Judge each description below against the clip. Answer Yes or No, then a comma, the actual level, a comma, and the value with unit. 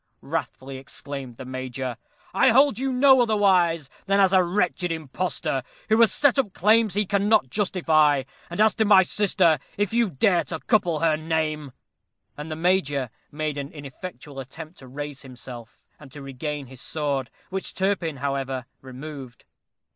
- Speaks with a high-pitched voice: No, medium, 155 Hz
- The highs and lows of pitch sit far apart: Yes, wide, 6.1 semitones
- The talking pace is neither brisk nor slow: Yes, average, 160 wpm